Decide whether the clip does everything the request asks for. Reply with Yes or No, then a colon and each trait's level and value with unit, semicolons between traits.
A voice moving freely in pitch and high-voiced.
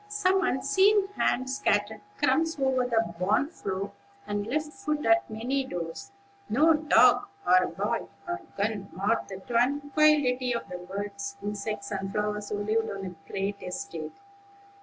Yes: wide, 6.8 semitones; high, 225 Hz